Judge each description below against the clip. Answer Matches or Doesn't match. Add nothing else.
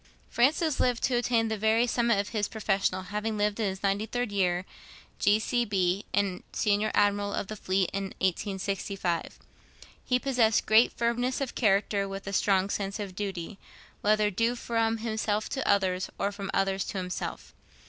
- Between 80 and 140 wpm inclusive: Doesn't match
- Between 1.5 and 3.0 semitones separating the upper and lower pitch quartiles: Matches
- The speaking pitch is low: Doesn't match